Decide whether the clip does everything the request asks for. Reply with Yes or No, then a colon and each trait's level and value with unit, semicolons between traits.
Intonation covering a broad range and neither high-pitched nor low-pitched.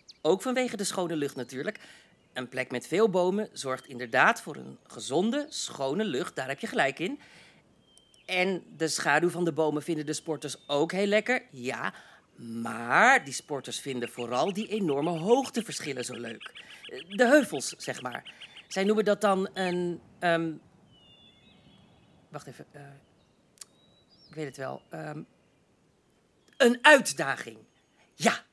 Yes: wide, 8.0 semitones; medium, 165 Hz